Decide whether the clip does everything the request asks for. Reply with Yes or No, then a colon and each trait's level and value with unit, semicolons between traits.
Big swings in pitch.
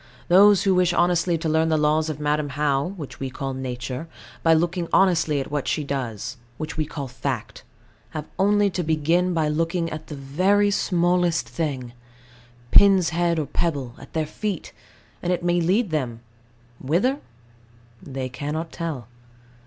No: average, 3.8 semitones